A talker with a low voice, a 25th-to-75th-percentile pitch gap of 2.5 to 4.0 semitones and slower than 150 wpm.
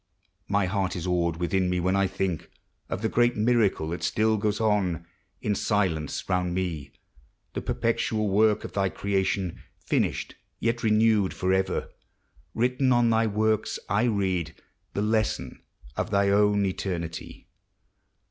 Yes: low, 100 Hz; average, 3.1 semitones; average, 140 wpm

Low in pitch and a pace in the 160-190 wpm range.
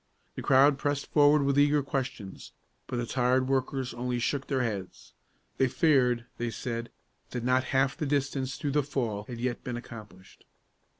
Yes: low, 130 Hz; average, 170 wpm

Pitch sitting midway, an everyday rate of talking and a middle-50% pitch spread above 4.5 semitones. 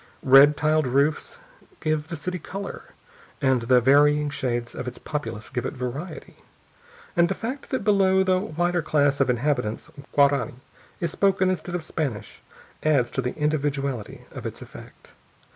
Yes: medium, 150 Hz; average, 155 wpm; average, 5.0 semitones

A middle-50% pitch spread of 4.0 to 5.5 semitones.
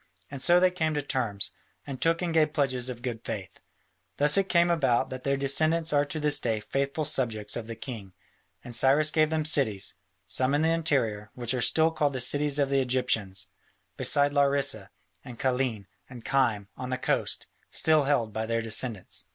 Yes: average, 4.5 semitones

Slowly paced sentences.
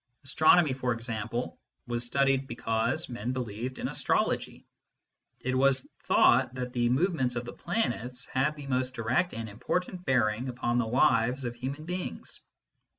No: average, 155 wpm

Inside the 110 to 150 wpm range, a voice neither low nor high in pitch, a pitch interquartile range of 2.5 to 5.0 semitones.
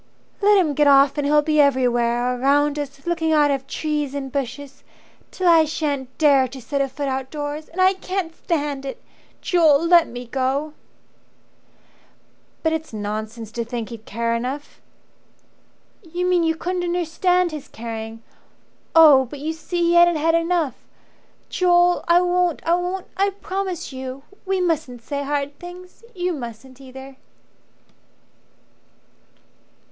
No: average, 145 wpm; very high, 295 Hz; average, 4.6 semitones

